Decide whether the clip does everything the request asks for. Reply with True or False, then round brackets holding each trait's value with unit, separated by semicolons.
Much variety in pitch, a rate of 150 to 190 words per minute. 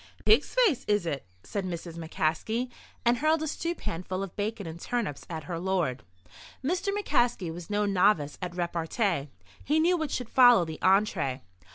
True (6.5 semitones; 170 wpm)